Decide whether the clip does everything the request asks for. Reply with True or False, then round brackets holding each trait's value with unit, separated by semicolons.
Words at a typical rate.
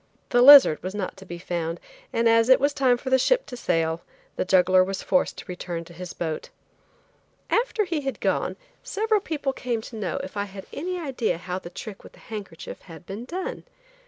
False (210 wpm)